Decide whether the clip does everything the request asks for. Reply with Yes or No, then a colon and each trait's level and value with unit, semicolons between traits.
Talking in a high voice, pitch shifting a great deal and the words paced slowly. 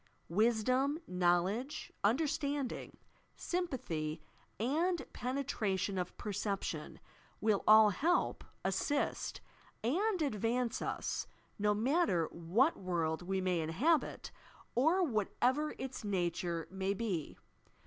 Yes: high, 215 Hz; wide, 7.2 semitones; slow, 95 wpm